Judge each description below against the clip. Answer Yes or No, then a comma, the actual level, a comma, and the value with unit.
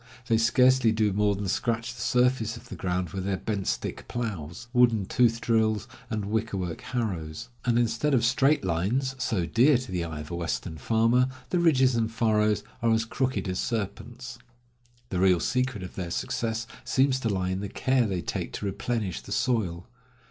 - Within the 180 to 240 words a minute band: Yes, average, 190 wpm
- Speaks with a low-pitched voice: Yes, low, 110 Hz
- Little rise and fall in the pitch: No, average, 4.4 semitones